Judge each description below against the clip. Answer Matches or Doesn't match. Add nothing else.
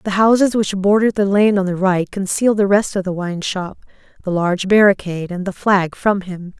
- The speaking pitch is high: Matches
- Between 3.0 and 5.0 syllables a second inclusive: Doesn't match